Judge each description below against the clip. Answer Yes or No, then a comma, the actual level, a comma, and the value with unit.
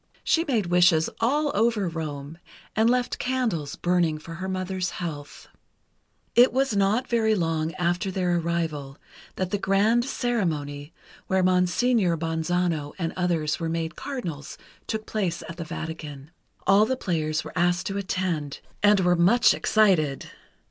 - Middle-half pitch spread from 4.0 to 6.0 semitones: Yes, average, 4.5 semitones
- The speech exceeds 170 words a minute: No, average, 145 wpm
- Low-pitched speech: No, medium, 180 Hz